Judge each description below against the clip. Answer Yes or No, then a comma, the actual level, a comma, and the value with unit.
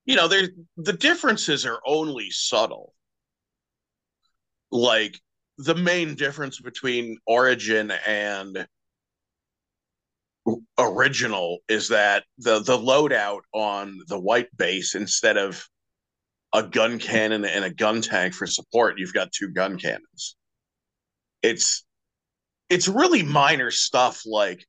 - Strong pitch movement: Yes, wide, 6.7 semitones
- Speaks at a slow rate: Yes, slow, 115 wpm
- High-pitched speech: No, low, 115 Hz